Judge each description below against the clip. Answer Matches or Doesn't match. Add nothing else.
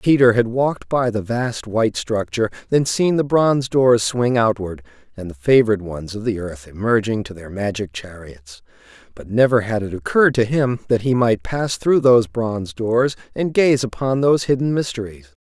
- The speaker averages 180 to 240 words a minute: Matches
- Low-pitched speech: Matches